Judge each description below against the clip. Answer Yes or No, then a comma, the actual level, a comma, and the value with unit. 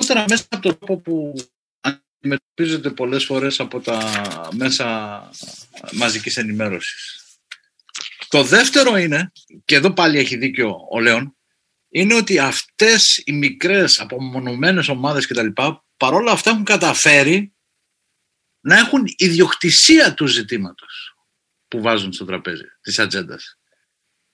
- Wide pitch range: Yes, wide, 8.1 semitones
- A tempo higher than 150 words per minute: No, slow, 115 wpm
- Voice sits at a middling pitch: Yes, medium, 150 Hz